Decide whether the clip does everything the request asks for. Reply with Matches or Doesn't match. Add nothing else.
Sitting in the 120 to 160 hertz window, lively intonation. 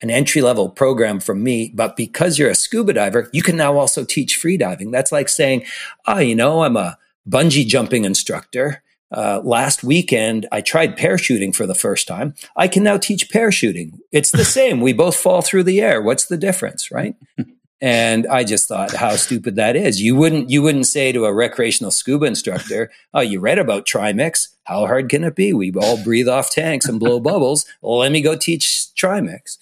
Matches